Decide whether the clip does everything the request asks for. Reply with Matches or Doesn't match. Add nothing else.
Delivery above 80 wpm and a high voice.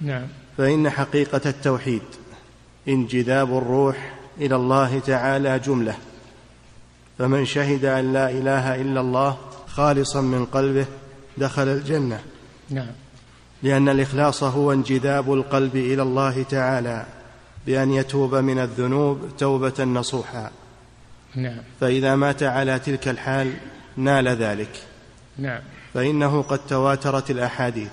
Doesn't match